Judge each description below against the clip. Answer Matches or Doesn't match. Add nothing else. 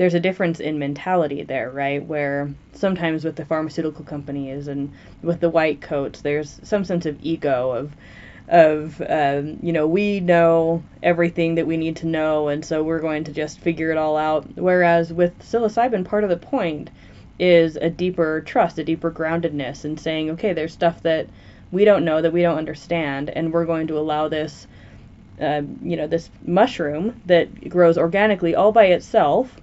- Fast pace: Doesn't match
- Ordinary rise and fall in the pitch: Doesn't match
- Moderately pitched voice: Matches